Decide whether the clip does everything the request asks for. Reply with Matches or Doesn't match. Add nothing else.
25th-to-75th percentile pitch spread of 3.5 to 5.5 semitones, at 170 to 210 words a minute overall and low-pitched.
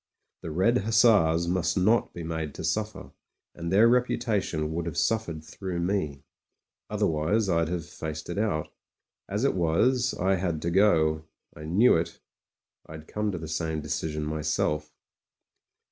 Doesn't match